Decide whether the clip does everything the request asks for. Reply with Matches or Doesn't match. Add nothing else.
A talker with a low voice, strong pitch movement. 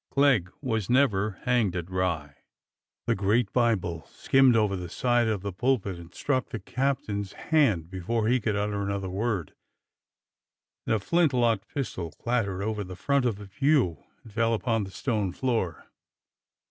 Doesn't match